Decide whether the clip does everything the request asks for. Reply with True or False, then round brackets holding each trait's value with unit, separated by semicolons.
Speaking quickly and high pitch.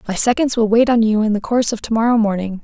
True (295 wpm; 225 Hz)